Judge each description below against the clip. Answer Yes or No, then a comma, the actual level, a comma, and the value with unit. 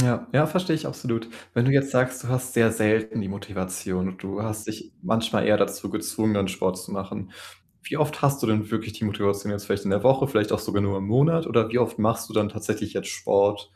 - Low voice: Yes, low, 110 Hz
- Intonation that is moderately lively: Yes, average, 3.8 semitones